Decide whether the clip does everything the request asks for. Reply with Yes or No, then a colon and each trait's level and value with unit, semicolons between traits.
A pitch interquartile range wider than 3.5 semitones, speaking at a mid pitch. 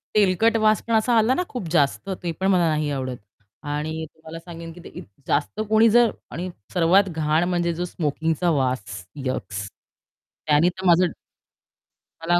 Yes: average, 3.9 semitones; medium, 170 Hz